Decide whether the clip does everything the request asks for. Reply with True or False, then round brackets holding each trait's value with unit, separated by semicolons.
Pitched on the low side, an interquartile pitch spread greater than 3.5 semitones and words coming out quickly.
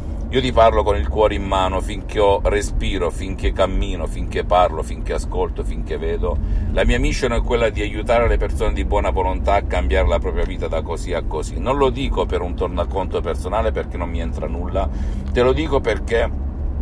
True (90 Hz; 4.6 semitones; 200 wpm)